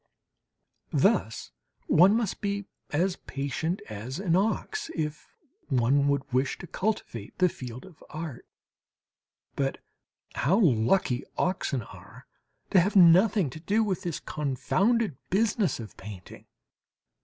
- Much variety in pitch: Yes, wide, 6.7 semitones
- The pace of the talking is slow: Yes, slow, 120 wpm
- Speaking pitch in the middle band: Yes, medium, 165 Hz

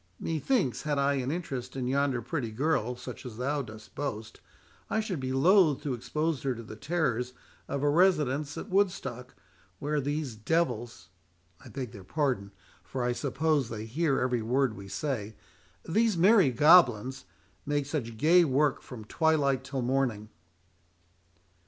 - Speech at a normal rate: Yes, average, 145 wpm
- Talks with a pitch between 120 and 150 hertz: Yes, low, 135 Hz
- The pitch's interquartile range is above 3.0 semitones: Yes, average, 4.3 semitones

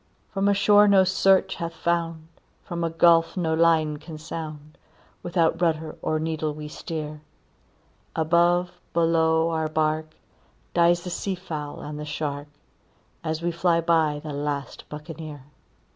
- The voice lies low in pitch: No, medium, 160 Hz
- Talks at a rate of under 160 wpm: Yes, average, 145 wpm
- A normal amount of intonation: No, narrow, 1.8 semitones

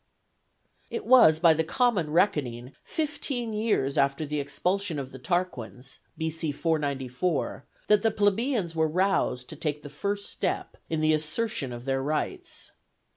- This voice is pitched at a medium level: Yes, medium, 160 Hz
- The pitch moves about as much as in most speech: No, wide, 6.5 semitones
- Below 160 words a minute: Yes, average, 150 wpm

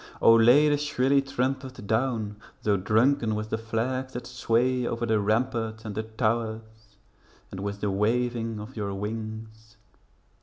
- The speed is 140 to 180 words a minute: Yes, average, 150 wpm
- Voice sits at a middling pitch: No, low, 115 Hz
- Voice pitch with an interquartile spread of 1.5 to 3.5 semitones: Yes, narrow, 2.5 semitones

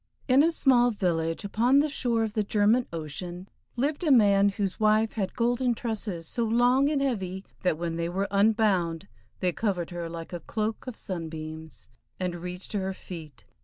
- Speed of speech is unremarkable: Yes, average, 180 wpm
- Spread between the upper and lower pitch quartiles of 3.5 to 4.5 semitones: No, average, 5.2 semitones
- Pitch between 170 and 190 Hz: No, high, 200 Hz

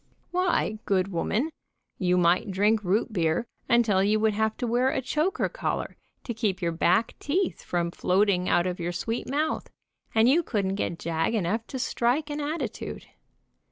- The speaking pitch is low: No, high, 215 Hz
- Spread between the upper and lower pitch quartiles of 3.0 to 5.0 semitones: No, wide, 5.6 semitones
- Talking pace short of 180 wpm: Yes, average, 170 wpm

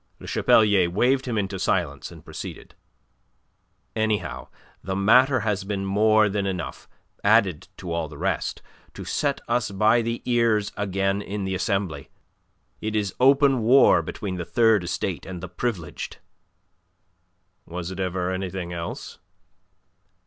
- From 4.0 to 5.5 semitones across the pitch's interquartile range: No, average, 3.1 semitones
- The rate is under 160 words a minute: Yes, average, 140 wpm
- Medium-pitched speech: No, low, 100 Hz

